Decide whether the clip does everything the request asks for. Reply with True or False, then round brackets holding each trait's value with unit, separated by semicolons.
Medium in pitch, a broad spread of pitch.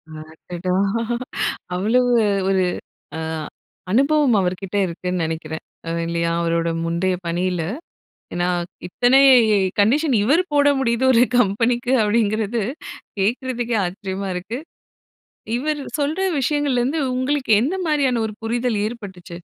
False (225 Hz; 6.1 semitones)